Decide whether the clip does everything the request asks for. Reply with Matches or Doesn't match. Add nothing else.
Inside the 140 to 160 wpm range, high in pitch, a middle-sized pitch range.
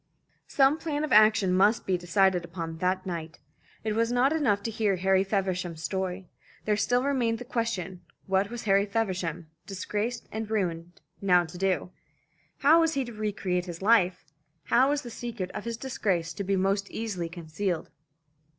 Doesn't match